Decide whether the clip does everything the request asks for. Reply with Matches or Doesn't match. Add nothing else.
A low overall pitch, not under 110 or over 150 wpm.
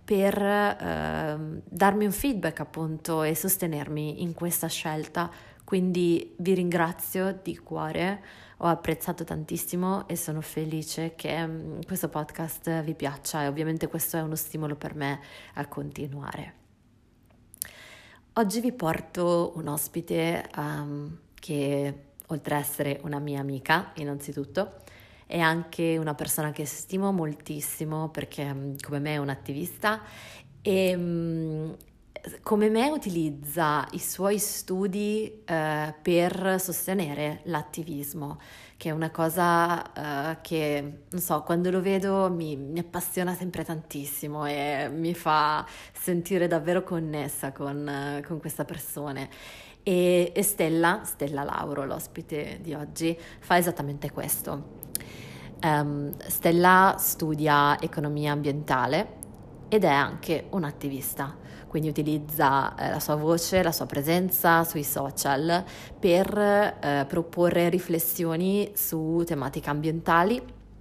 Doesn't match